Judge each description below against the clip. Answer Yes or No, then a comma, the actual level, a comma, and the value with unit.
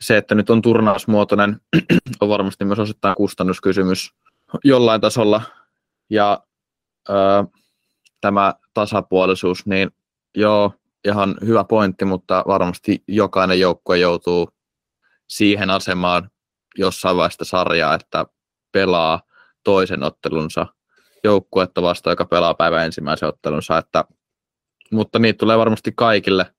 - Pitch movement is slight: Yes, narrow, 2.3 semitones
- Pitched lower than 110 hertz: Yes, low, 100 Hz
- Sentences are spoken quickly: No, average, 110 wpm